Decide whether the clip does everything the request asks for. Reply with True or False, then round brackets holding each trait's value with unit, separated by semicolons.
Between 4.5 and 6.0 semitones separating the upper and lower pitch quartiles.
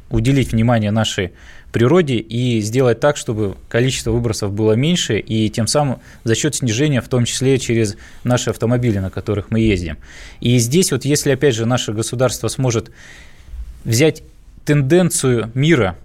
False (3.4 semitones)